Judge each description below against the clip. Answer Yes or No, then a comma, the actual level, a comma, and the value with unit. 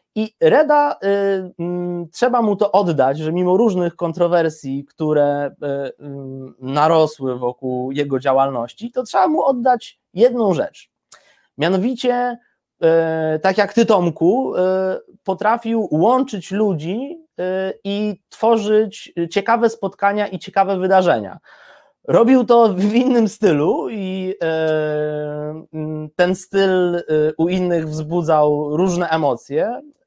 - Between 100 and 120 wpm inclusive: Yes, average, 115 wpm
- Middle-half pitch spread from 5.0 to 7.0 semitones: Yes, wide, 5.5 semitones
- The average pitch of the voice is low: No, medium, 185 Hz